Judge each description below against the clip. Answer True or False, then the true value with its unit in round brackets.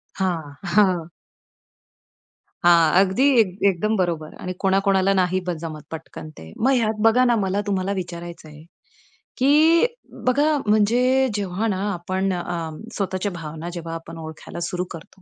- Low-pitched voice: False (185 Hz)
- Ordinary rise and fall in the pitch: True (3.4 semitones)